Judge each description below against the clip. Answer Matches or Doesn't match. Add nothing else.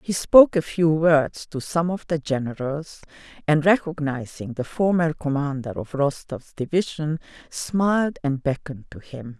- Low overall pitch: Doesn't match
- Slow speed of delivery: Doesn't match